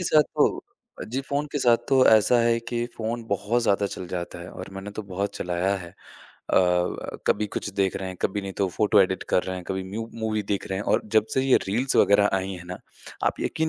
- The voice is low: Yes, low, 100 Hz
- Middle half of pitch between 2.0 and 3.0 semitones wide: No, average, 3.6 semitones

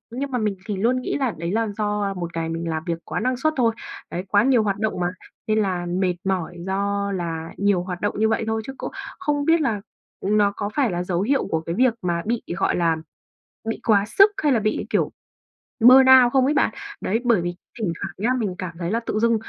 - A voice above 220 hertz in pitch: No, high, 205 Hz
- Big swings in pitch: No, average, 4.8 semitones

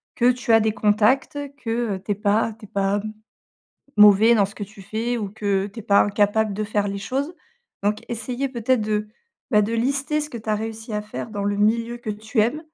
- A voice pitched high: Yes, high, 215 Hz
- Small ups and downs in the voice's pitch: Yes, narrow, 2.3 semitones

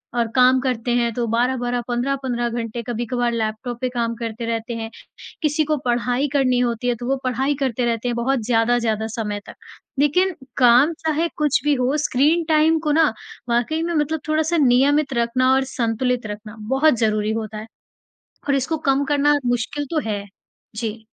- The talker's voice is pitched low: No, high, 245 Hz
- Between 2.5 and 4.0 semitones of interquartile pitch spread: Yes, average, 3.5 semitones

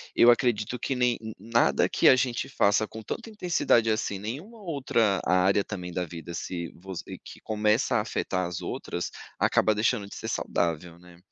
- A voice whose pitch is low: Yes, low, 105 Hz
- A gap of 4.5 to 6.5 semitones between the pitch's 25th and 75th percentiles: Yes, average, 5.1 semitones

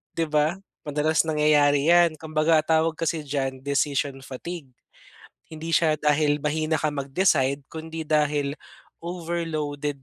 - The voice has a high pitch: No, medium, 155 Hz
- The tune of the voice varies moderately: No, narrow, 1.9 semitones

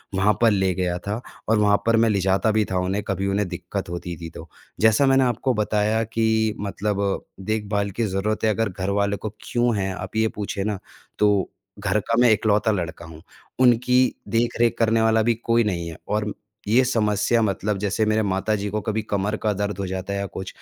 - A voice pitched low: Yes, low, 105 Hz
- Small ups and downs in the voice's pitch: Yes, narrow, 2.3 semitones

